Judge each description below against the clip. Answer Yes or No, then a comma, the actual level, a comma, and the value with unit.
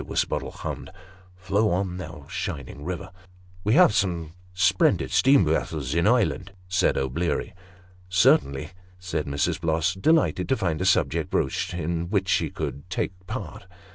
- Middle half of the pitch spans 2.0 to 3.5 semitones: Yes, average, 2.8 semitones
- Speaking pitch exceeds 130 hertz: No, very low, 90 Hz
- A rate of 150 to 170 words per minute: Yes, average, 155 wpm